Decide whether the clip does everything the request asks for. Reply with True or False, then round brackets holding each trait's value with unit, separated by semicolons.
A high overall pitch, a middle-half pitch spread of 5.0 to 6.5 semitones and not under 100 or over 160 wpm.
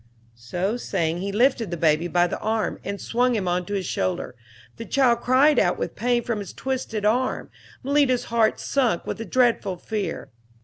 False (220 Hz; 5.5 semitones; 185 wpm)